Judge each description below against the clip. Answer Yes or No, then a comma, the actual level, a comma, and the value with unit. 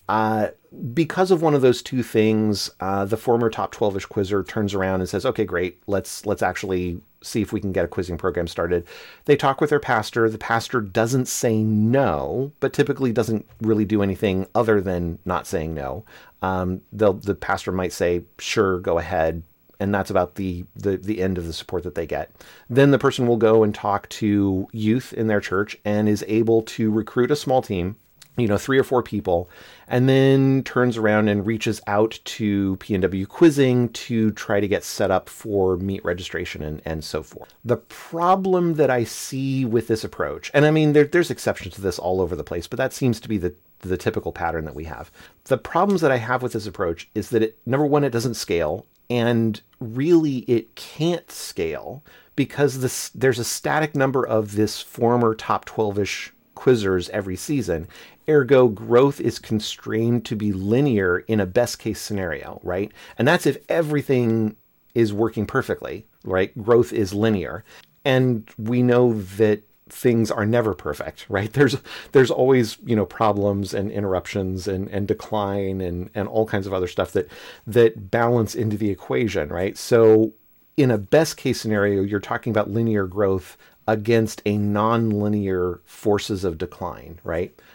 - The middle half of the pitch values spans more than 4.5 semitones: No, average, 3.9 semitones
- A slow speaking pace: No, average, 185 wpm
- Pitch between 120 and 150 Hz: No, low, 110 Hz